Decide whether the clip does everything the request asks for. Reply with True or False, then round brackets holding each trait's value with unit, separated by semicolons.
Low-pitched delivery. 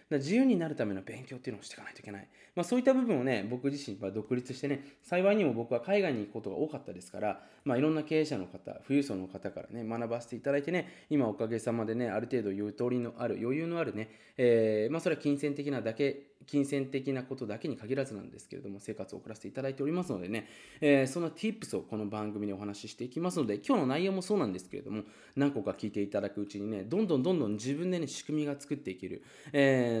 True (130 Hz)